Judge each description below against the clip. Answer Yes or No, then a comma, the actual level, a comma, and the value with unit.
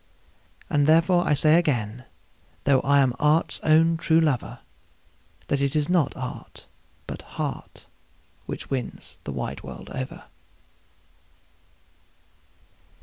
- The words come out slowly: Yes, slow, 115 wpm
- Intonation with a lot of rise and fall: No, average, 3.7 semitones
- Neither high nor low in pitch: Yes, medium, 145 Hz